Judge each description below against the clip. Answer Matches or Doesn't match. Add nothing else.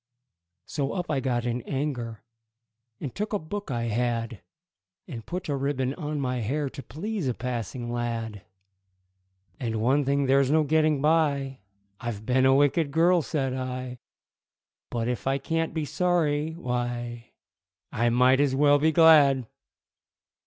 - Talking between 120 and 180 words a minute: Matches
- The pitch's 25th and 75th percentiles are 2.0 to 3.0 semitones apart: Doesn't match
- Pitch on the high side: Doesn't match